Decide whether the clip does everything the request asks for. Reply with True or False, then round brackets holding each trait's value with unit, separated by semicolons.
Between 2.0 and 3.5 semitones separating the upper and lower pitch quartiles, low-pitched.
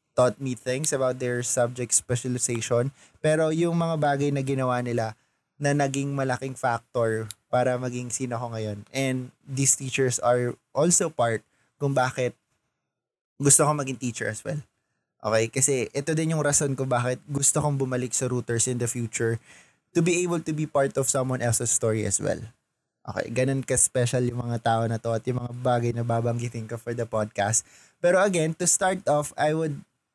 True (3.0 semitones; 125 Hz)